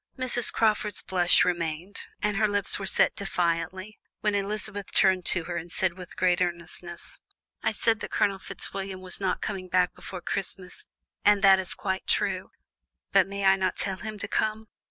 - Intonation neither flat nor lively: No, narrow, 2.1 semitones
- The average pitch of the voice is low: No, high, 190 Hz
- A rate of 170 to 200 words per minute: Yes, average, 180 wpm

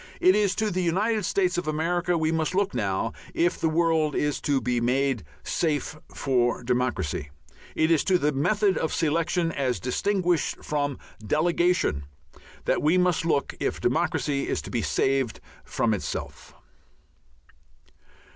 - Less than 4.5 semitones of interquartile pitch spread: No, average, 5.1 semitones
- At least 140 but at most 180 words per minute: Yes, average, 145 wpm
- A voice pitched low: No, medium, 155 Hz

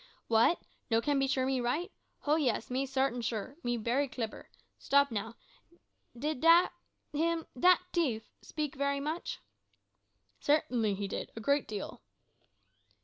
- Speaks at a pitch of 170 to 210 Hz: No, very high, 265 Hz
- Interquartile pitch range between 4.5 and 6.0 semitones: No, average, 4.1 semitones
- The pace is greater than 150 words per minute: No, average, 140 wpm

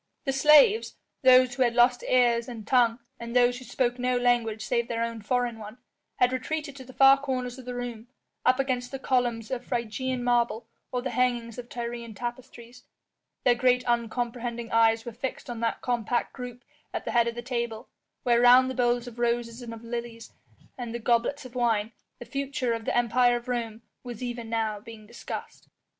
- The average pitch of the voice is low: No, high, 240 Hz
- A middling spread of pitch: No, narrow, 1.4 semitones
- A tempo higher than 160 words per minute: Yes, average, 195 wpm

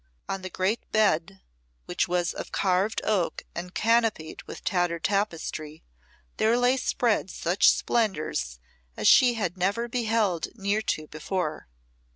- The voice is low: No, high, 195 Hz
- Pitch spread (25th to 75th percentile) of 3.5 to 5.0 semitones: Yes, average, 4.3 semitones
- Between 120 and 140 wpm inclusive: Yes, slow, 135 wpm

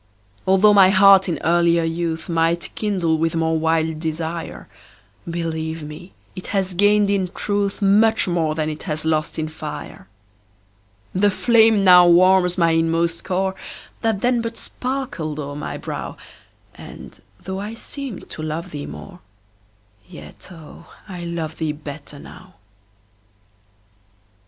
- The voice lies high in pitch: No, medium, 170 Hz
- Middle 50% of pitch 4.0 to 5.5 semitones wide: No, average, 3.4 semitones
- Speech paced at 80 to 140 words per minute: Yes, slow, 135 wpm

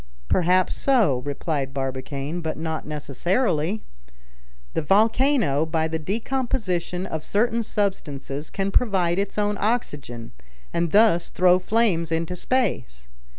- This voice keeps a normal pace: No, slow, 115 wpm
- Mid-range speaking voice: Yes, medium, 175 Hz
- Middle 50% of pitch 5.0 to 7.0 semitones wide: Yes, wide, 5.5 semitones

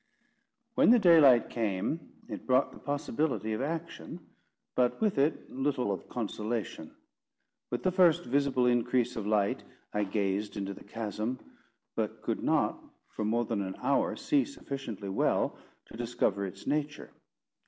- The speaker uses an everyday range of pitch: No, wide, 5.7 semitones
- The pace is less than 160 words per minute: Yes, average, 145 wpm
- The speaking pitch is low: Yes, low, 120 Hz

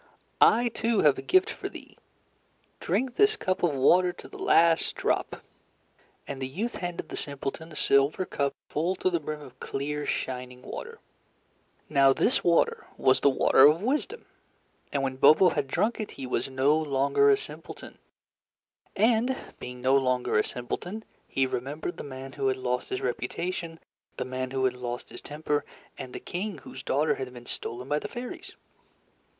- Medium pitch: Yes, medium, 145 Hz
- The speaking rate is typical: Yes, average, 175 wpm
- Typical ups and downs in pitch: No, wide, 6.0 semitones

